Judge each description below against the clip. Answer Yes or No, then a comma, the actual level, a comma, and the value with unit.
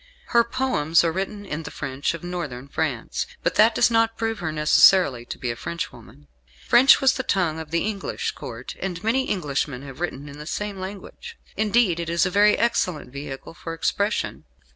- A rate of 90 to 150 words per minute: No, average, 190 wpm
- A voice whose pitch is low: No, medium, 175 Hz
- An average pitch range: No, wide, 5.9 semitones